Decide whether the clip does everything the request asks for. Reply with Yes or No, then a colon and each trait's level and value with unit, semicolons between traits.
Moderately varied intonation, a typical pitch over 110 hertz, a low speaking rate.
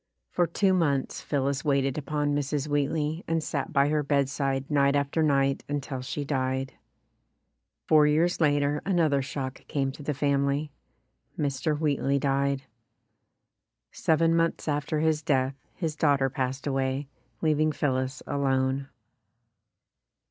No: narrow, 1.9 semitones; medium, 140 Hz; slow, 130 wpm